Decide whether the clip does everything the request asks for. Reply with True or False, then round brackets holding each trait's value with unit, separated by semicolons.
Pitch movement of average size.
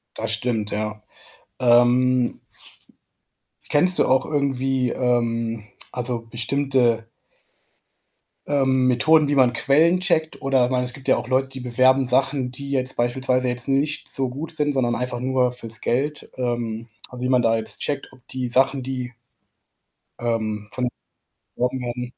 False (2.0 semitones)